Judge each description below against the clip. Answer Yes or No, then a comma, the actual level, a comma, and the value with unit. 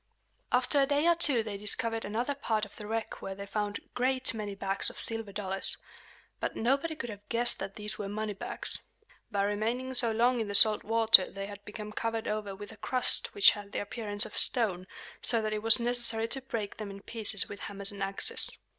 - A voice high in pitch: Yes, high, 215 Hz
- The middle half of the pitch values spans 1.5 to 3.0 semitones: Yes, average, 2.7 semitones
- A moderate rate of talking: No, fast, 215 wpm